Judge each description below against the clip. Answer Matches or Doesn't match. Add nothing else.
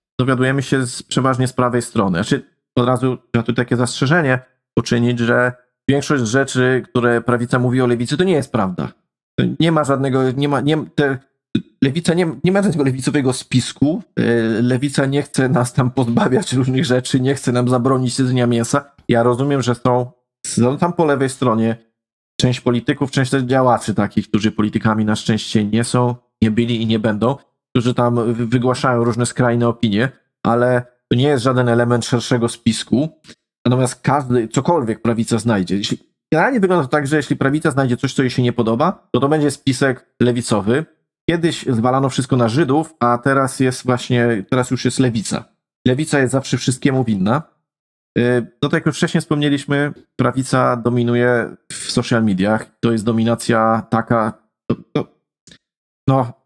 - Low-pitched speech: Matches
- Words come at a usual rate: Doesn't match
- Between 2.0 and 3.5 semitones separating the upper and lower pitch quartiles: Matches